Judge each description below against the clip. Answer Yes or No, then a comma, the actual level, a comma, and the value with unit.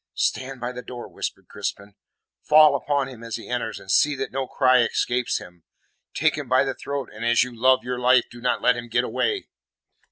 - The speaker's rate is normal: No, fast, 215 wpm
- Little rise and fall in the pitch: Yes, narrow, 2.1 semitones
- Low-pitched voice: Yes, low, 125 Hz